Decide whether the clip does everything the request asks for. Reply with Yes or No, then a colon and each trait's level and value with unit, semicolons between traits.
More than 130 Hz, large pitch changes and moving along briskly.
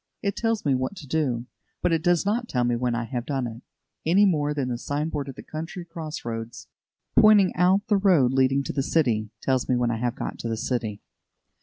Yes: medium, 140 Hz; wide, 6.2 semitones; fast, 230 wpm